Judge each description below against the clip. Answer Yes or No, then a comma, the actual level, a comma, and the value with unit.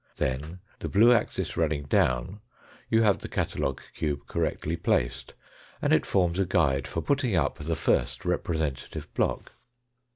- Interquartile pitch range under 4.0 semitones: No, average, 5.3 semitones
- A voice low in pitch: Yes, very low, 80 Hz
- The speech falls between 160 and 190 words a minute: No, average, 150 wpm